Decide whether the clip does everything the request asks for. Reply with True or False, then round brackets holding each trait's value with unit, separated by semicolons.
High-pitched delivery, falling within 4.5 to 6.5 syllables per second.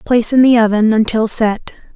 True (225 Hz; 5.5 syllables/s)